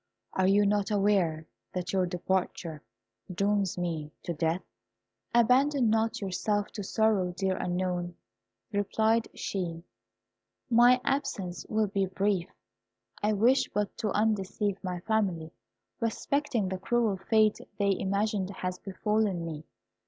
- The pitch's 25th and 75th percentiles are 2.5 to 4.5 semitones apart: Yes, average, 3.1 semitones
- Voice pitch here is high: Yes, high, 200 Hz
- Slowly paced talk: Yes, slow, 125 wpm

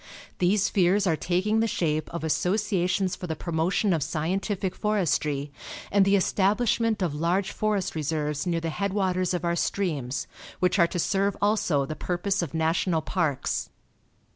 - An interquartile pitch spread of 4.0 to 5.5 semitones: No, average, 3.6 semitones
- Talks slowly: No, average, 155 wpm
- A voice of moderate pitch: Yes, medium, 180 Hz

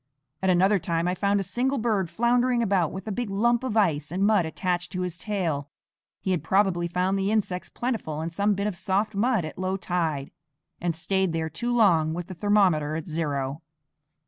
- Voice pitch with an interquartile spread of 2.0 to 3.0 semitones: No, average, 4.0 semitones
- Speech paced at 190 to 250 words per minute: Yes, average, 200 wpm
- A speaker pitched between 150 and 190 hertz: Yes, medium, 185 Hz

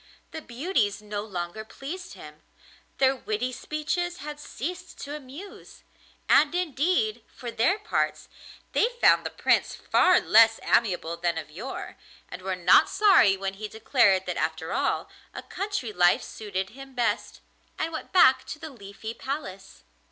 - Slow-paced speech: No, average, 150 wpm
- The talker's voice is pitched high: Yes, high, 240 Hz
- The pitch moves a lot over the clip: Yes, wide, 8.1 semitones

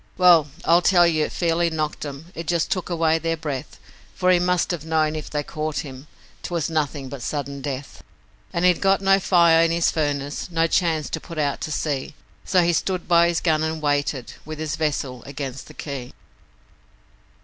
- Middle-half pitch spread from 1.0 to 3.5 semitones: Yes, average, 2.8 semitones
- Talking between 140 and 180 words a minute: No, average, 195 wpm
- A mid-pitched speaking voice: Yes, medium, 160 Hz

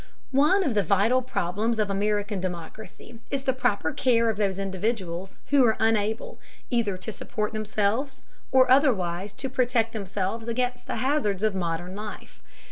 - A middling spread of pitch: Yes, average, 4.0 semitones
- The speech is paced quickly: No, average, 155 wpm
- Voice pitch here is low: No, high, 215 Hz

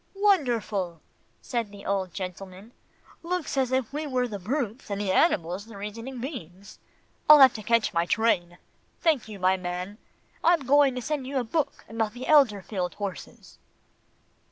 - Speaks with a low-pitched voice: No, high, 225 Hz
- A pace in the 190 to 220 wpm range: No, average, 160 wpm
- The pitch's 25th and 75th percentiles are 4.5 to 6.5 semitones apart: Yes, wide, 5.5 semitones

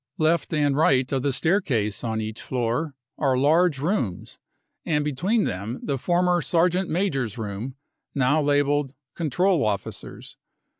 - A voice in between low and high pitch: Yes, medium, 145 Hz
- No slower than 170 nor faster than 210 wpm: No, average, 145 wpm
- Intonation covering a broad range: No, average, 5.0 semitones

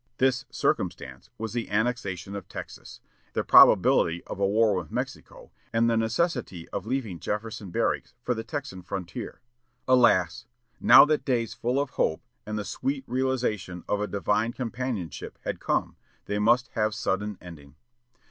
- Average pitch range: Yes, average, 4.6 semitones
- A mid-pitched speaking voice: No, low, 110 Hz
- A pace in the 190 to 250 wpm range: No, average, 155 wpm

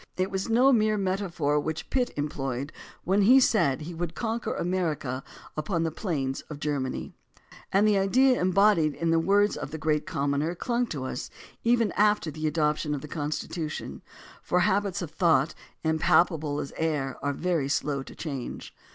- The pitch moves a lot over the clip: No, average, 4.9 semitones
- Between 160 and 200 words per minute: Yes, average, 175 wpm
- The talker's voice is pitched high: No, medium, 165 Hz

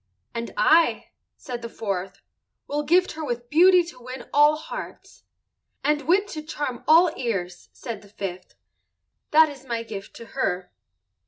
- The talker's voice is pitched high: Yes, very high, 255 Hz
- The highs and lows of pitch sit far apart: Yes, wide, 5.7 semitones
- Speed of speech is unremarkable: Yes, average, 155 wpm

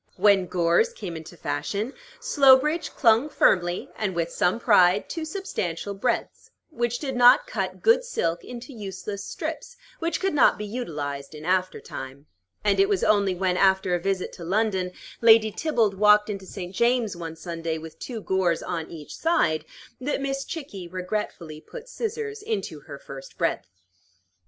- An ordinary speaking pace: Yes, average, 160 wpm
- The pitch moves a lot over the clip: Yes, wide, 7.0 semitones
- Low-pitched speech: No, high, 200 Hz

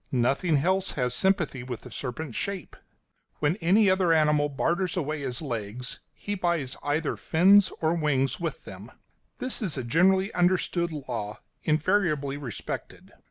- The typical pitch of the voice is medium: Yes, medium, 155 Hz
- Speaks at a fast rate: No, average, 145 wpm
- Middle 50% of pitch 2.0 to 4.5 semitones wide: No, average, 5.2 semitones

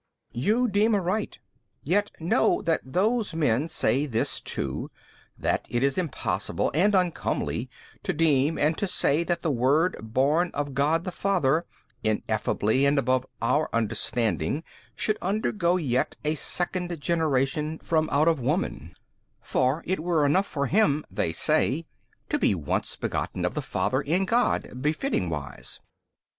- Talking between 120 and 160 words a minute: Yes, average, 150 wpm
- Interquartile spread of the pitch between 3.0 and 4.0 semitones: No, average, 5.1 semitones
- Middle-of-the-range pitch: Yes, medium, 155 Hz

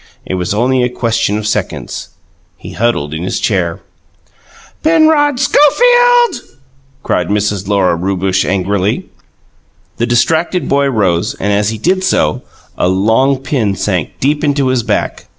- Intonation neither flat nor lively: No, wide, 6.9 semitones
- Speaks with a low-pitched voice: Yes, low, 110 Hz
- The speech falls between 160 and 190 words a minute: No, average, 140 wpm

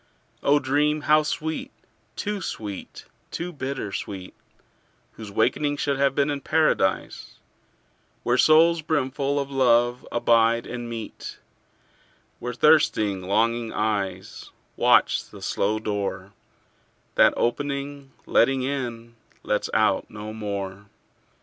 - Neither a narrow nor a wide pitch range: Yes, average, 4.9 semitones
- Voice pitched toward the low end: Yes, low, 120 Hz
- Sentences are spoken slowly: Yes, slow, 110 wpm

